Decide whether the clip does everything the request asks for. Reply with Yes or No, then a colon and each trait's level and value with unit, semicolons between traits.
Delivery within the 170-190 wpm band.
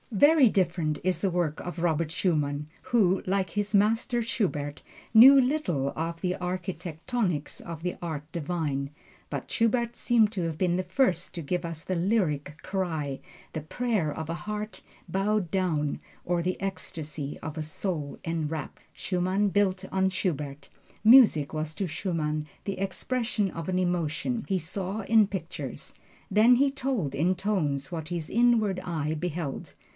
No: average, 155 wpm